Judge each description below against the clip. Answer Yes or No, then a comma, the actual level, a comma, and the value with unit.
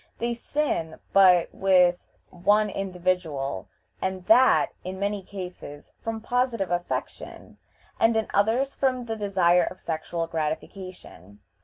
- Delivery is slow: Yes, slow, 120 wpm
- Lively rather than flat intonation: No, average, 4.1 semitones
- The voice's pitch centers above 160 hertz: Yes, high, 190 Hz